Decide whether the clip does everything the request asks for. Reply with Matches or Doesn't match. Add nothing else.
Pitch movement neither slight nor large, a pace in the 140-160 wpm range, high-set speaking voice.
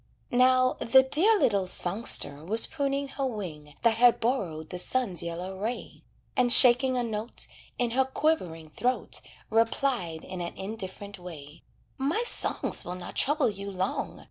Doesn't match